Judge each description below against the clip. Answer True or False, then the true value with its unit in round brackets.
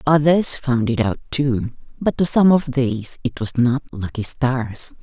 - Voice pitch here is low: True (130 Hz)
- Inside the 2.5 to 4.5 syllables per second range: True (4.1 syllables/s)